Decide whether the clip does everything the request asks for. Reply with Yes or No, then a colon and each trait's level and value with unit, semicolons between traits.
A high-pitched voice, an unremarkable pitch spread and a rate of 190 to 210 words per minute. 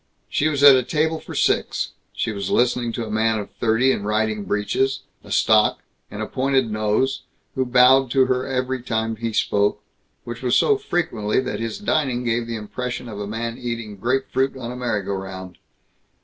No: low, 120 Hz; average, 3.3 semitones; average, 195 wpm